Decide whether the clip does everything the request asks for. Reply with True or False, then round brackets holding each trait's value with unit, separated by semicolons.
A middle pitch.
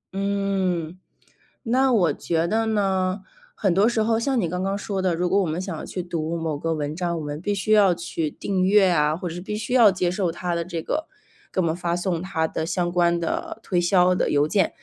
True (180 Hz)